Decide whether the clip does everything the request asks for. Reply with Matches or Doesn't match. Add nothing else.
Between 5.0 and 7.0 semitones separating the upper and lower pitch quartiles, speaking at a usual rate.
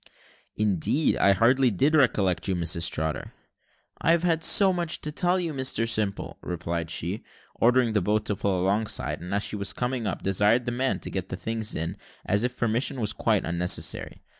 Matches